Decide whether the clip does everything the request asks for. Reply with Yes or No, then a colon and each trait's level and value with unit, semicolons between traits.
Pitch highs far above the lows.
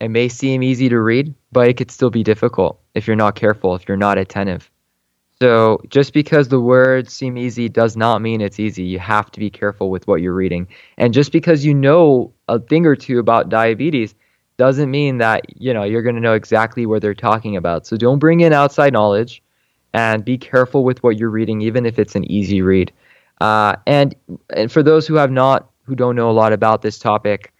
No: average, 3.5 semitones